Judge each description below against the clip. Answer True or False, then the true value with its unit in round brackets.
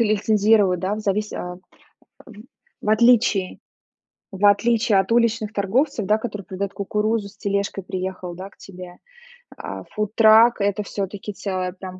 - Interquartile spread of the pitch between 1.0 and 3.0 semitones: True (2.4 semitones)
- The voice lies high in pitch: True (205 Hz)